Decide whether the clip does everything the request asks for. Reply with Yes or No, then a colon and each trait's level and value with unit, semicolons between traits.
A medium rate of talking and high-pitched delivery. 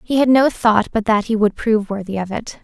No: fast, 275 wpm; high, 220 Hz